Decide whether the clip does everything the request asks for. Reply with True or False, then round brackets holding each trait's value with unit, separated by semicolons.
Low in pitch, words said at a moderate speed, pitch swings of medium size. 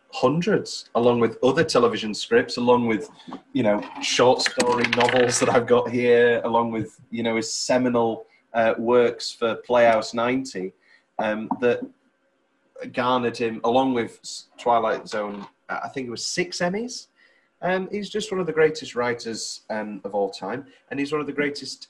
True (120 Hz; 165 wpm; 3.8 semitones)